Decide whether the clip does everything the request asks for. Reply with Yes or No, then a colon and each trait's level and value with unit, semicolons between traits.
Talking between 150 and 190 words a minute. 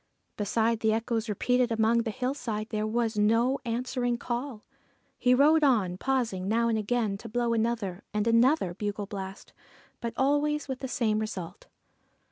Yes: average, 155 wpm